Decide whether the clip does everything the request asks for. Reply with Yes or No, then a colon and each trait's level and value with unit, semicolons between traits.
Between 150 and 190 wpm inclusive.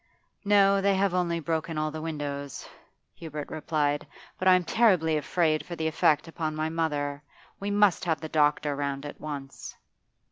Yes: average, 170 wpm